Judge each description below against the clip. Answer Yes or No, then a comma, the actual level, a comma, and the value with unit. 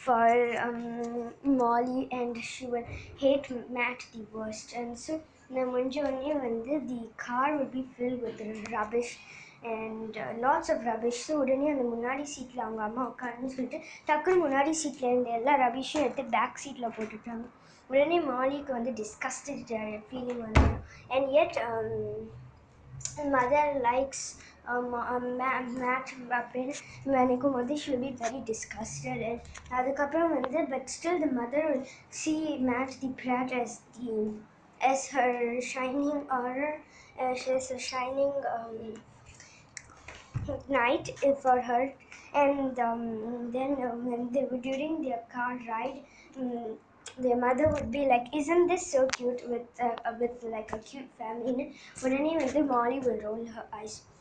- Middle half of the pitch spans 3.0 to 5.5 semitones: No, narrow, 2.5 semitones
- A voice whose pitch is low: No, very high, 250 Hz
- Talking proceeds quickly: Yes, fast, 150 wpm